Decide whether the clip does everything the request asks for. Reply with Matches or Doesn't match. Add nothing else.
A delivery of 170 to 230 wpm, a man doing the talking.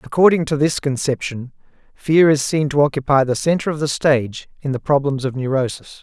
Matches